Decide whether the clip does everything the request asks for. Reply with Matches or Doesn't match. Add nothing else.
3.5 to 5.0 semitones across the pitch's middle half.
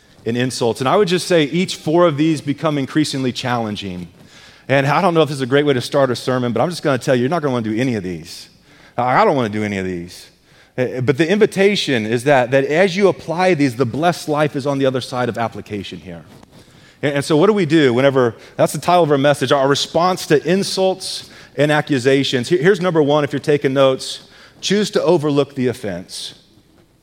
Matches